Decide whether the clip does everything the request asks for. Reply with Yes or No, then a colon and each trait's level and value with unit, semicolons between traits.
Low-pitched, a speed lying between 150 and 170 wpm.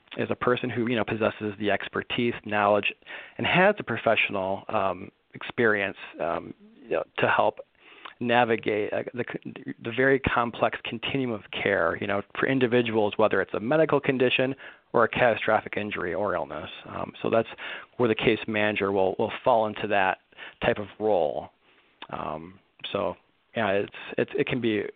Yes: low, 115 Hz; average, 160 wpm